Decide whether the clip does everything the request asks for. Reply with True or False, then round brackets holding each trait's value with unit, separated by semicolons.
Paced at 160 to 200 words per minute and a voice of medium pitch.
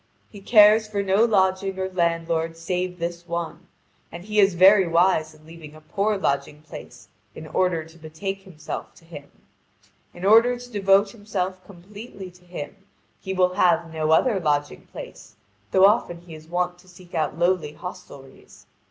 True (170 wpm; 180 Hz)